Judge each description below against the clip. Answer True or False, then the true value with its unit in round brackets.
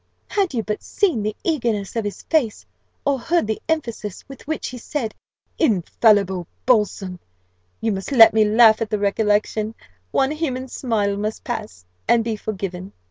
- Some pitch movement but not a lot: True (3.7 semitones)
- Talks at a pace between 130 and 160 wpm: True (155 wpm)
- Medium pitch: False (220 Hz)